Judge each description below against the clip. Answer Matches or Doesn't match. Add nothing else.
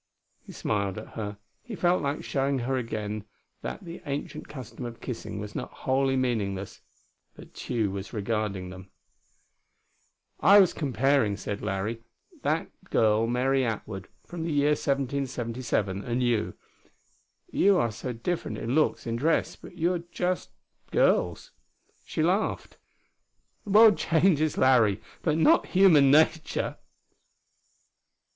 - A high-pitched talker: Doesn't match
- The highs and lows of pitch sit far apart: Matches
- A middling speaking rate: Doesn't match